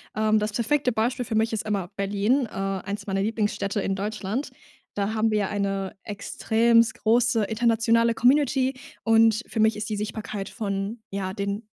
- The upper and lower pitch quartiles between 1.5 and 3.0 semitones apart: Yes, narrow, 2.5 semitones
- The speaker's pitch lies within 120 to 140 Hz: No, high, 215 Hz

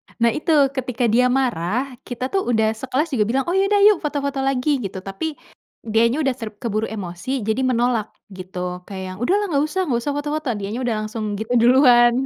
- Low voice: No, very high, 250 Hz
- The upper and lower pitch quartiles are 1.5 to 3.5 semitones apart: No, average, 4.1 semitones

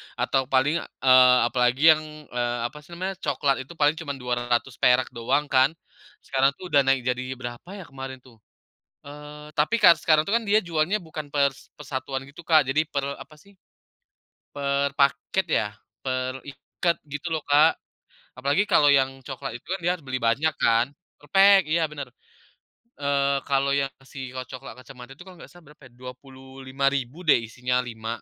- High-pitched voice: No, medium, 140 Hz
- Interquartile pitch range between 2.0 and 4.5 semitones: Yes, average, 2.9 semitones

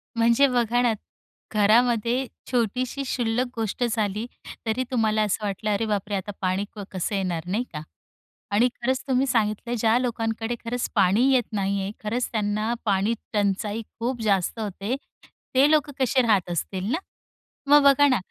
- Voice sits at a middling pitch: No, high, 225 Hz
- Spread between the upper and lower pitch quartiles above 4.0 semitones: No, average, 3.2 semitones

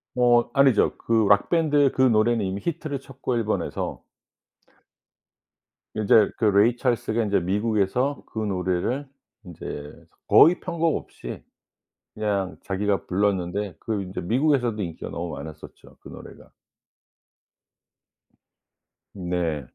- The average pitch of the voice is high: No, low, 105 Hz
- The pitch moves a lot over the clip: No, average, 4.8 semitones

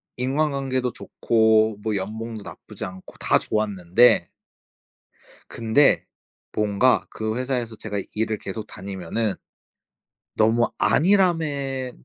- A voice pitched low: Yes, low, 110 Hz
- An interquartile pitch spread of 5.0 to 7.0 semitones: No, average, 3.4 semitones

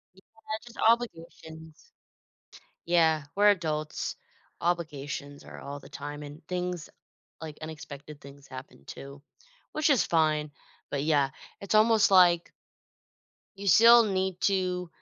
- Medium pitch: Yes, medium, 165 Hz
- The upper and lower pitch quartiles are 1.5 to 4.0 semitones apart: No, average, 4.4 semitones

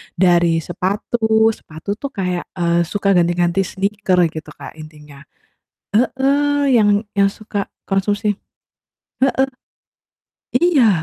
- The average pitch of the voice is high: Yes, high, 195 Hz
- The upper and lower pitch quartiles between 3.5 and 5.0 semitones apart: Yes, average, 4.2 semitones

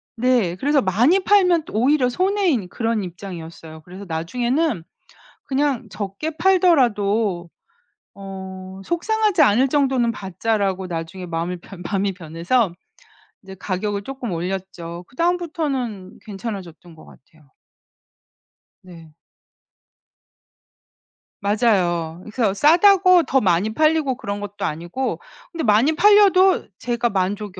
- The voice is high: Yes, high, 210 Hz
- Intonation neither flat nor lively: No, wide, 7.2 semitones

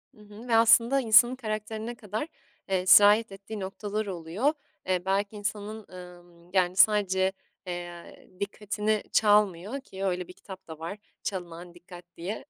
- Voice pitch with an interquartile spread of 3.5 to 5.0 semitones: No, average, 3.1 semitones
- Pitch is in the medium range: No, high, 200 Hz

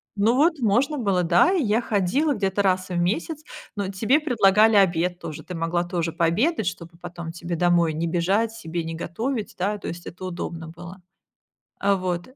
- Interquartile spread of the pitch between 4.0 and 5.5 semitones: Yes, average, 4.3 semitones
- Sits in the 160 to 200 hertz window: Yes, medium, 185 Hz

